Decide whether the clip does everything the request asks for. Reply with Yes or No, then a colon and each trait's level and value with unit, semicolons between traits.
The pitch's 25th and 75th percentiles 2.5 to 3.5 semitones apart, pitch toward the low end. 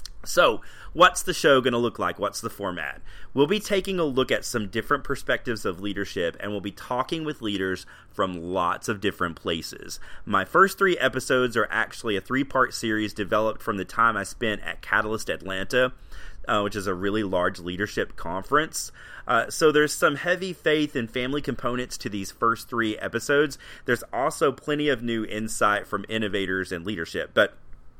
No: wide, 5.4 semitones; low, 115 Hz